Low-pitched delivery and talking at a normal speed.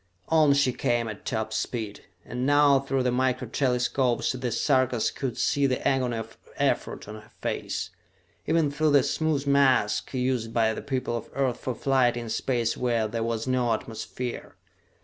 Yes: low, 125 Hz; average, 170 wpm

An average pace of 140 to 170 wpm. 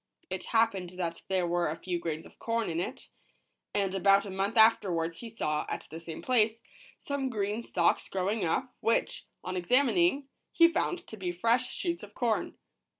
No: average, 180 wpm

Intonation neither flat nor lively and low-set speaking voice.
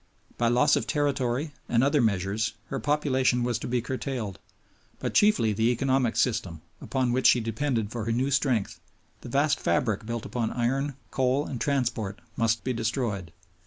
Yes: average, 3.0 semitones; low, 120 Hz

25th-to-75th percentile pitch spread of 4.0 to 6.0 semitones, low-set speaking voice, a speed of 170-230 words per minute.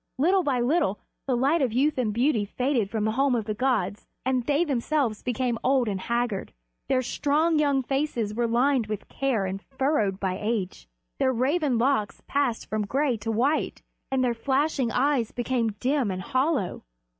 No: average, 4.3 semitones; very high, 250 Hz; average, 180 wpm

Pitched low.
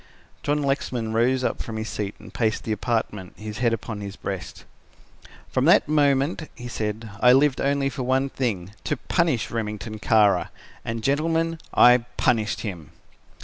Yes: low, 120 Hz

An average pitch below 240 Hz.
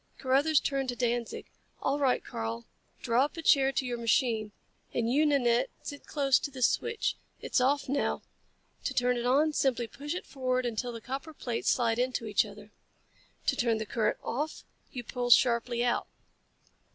No: very high, 250 Hz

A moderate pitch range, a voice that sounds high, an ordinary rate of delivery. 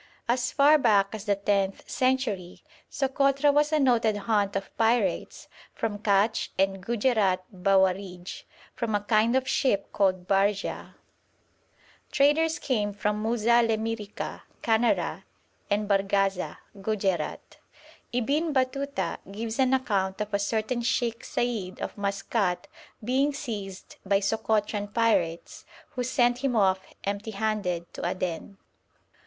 No: average, 3.7 semitones; high, 215 Hz; slow, 125 wpm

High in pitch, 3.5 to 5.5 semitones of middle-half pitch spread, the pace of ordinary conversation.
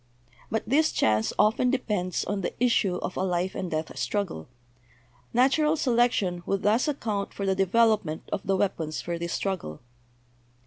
Yes: high, 195 Hz; average, 4.7 semitones; average, 170 wpm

